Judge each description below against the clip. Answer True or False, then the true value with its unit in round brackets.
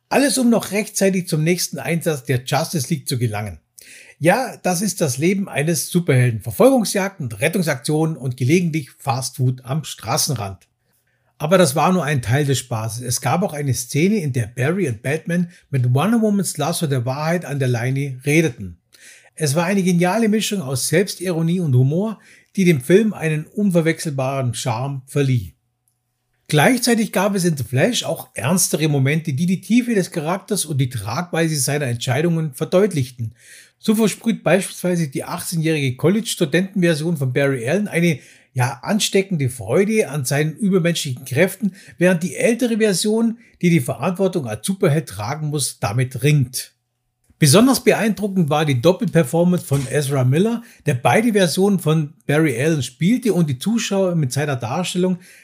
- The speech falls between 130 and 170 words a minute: True (155 wpm)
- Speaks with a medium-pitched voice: True (160 Hz)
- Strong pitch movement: True (5.7 semitones)